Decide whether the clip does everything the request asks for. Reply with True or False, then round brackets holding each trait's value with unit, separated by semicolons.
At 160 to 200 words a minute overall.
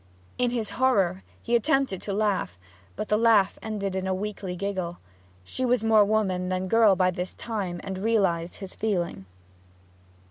True (165 wpm)